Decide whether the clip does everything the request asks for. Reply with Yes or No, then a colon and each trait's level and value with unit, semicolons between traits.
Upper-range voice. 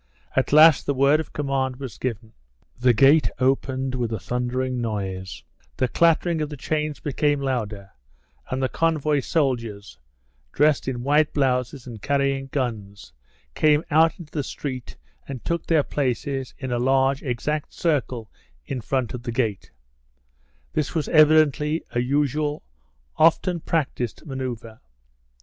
No: low, 135 Hz